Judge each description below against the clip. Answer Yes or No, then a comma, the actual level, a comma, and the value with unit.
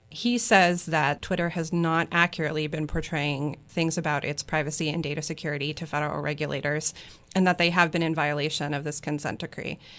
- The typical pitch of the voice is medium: Yes, medium, 155 Hz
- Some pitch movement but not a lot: No, narrow, 2.3 semitones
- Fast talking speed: No, average, 180 wpm